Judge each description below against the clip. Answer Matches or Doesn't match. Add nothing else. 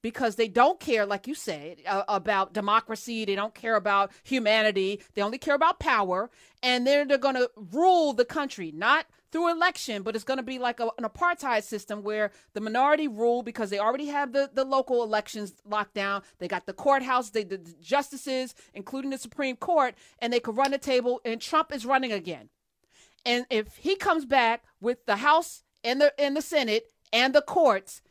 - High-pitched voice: Matches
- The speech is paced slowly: Doesn't match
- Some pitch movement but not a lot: Matches